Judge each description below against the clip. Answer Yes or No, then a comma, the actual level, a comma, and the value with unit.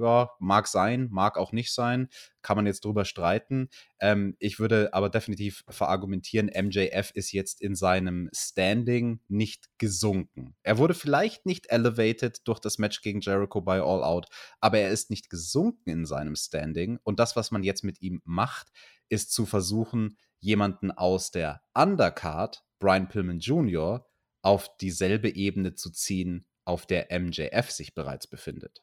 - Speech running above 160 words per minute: No, average, 155 wpm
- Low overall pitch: Yes, low, 100 Hz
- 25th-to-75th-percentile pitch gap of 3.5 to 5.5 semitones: No, average, 3.0 semitones